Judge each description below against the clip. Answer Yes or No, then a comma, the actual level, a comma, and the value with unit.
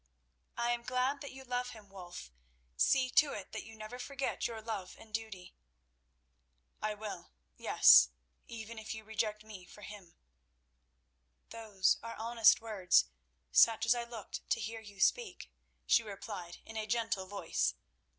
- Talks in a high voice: Yes, high, 220 Hz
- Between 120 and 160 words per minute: Yes, average, 150 wpm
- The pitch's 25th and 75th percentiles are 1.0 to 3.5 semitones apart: Yes, average, 2.8 semitones